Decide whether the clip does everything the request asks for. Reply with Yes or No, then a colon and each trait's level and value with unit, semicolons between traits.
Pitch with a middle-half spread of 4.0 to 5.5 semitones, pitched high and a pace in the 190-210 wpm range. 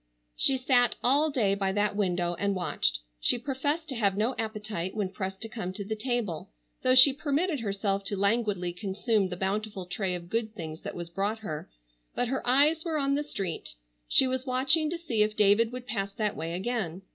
Yes: average, 5.0 semitones; high, 215 Hz; fast, 205 wpm